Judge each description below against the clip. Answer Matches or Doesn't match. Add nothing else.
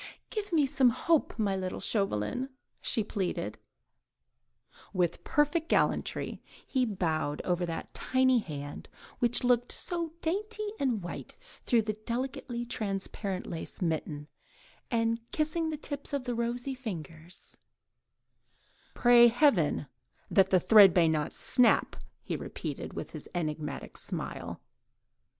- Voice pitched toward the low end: Doesn't match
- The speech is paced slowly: Matches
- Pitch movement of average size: Doesn't match